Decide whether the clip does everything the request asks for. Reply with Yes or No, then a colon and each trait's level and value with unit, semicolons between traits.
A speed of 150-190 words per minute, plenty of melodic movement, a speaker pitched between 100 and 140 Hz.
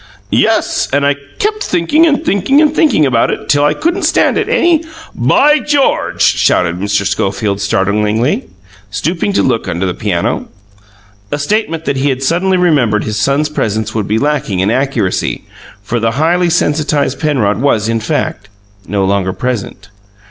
Yes: average, 165 wpm; wide, 8.9 semitones; low, 135 Hz